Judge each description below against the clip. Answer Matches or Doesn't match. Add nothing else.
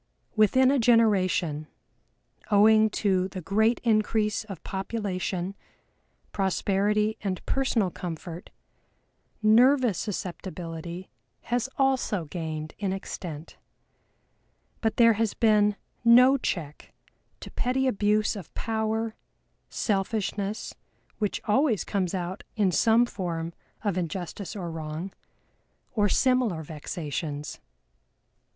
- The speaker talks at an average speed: Doesn't match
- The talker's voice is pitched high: Matches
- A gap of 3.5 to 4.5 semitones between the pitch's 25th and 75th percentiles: Matches